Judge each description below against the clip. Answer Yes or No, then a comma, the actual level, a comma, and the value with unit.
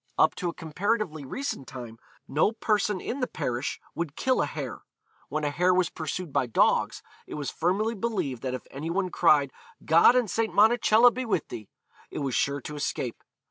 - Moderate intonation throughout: No, wide, 7.1 semitones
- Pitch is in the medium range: Yes, medium, 170 Hz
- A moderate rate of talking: Yes, average, 190 wpm